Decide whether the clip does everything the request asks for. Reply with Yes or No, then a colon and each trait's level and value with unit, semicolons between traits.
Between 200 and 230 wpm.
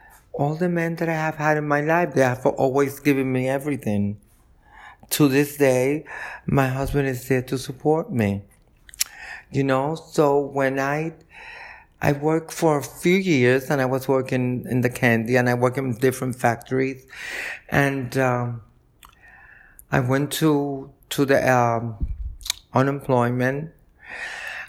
No: average, 145 wpm